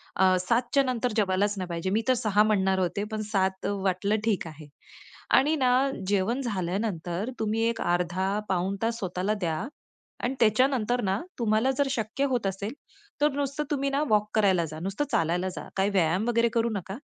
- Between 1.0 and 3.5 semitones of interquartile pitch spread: No, average, 3.9 semitones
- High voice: Yes, high, 205 Hz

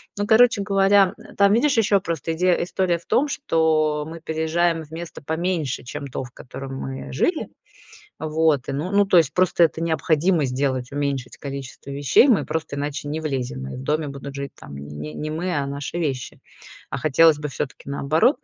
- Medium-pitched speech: Yes, medium, 155 Hz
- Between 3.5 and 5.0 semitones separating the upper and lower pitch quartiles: Yes, average, 4.1 semitones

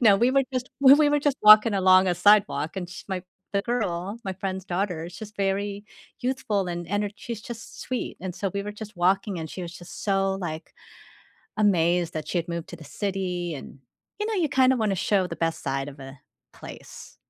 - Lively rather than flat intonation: No, average, 3.4 semitones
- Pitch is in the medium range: No, high, 195 Hz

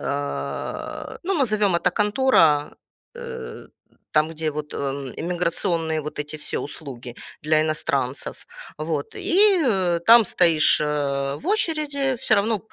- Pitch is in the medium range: Yes, medium, 165 Hz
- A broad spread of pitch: Yes, wide, 8.2 semitones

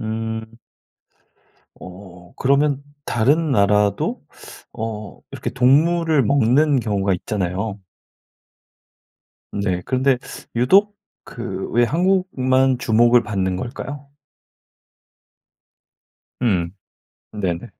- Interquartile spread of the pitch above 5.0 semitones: Yes, wide, 5.5 semitones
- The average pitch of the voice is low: Yes, low, 120 Hz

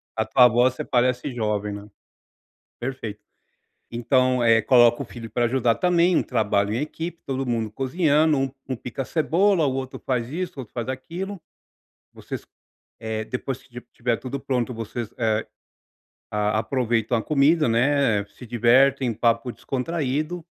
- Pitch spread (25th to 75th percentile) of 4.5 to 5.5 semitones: No, average, 3.3 semitones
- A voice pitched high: No, low, 125 Hz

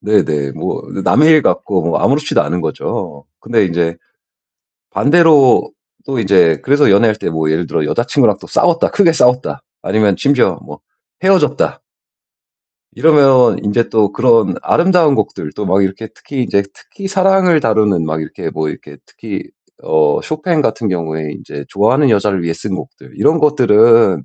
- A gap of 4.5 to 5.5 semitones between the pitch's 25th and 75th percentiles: No, wide, 9.0 semitones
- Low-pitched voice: Yes, low, 110 Hz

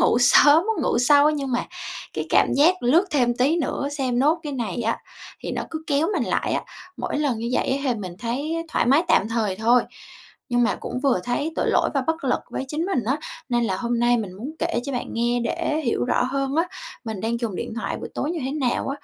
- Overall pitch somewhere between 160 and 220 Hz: No, very high, 255 Hz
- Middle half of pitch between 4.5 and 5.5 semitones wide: No, average, 3.8 semitones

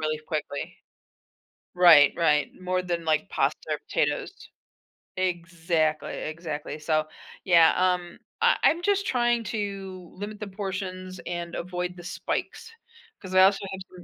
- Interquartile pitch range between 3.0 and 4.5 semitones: No, narrow, 2.6 semitones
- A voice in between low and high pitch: Yes, medium, 180 Hz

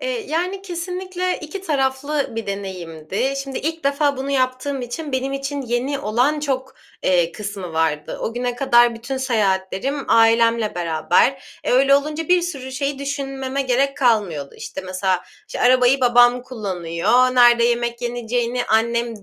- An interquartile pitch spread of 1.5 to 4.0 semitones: Yes, average, 3.6 semitones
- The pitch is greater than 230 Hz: Yes, very high, 250 Hz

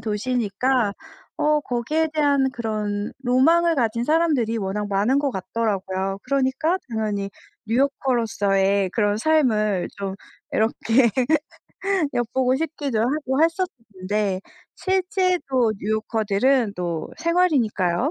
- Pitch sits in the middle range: No, high, 235 Hz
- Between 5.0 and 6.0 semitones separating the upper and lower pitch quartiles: Yes, wide, 5.4 semitones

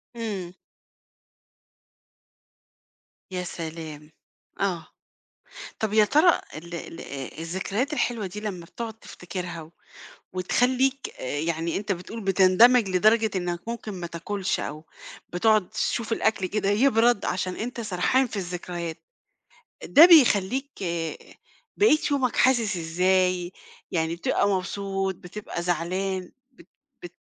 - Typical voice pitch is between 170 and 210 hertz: Yes, high, 190 Hz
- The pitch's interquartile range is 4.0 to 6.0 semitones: Yes, average, 4.4 semitones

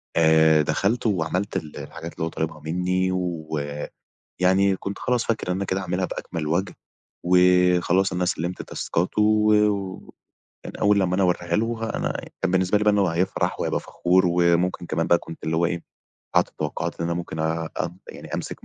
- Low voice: Yes, very low, 90 Hz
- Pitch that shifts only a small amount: Yes, narrow, 2.3 semitones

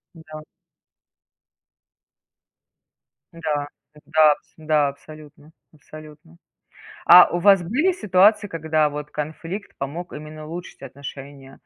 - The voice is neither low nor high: Yes, medium, 155 Hz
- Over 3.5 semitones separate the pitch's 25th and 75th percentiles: No, average, 2.7 semitones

